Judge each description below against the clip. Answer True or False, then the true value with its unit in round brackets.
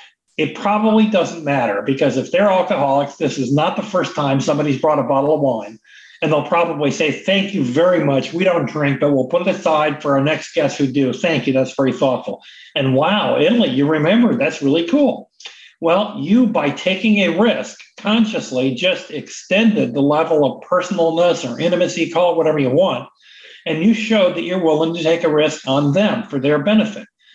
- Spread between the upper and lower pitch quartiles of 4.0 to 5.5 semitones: True (5.1 semitones)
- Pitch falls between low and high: True (160 Hz)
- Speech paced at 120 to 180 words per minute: False (195 wpm)